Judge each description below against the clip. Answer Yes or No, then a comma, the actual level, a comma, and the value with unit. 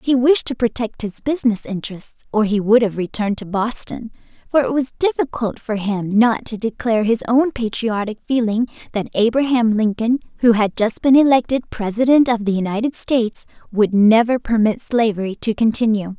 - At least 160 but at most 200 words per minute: Yes, average, 170 wpm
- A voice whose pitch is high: Yes, high, 230 Hz